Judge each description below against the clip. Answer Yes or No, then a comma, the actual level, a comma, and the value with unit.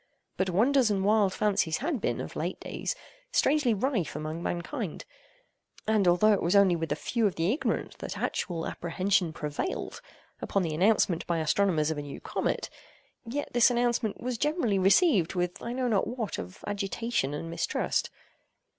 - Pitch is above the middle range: Yes, high, 200 Hz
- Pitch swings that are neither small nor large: No, wide, 5.7 semitones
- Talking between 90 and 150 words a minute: No, average, 170 wpm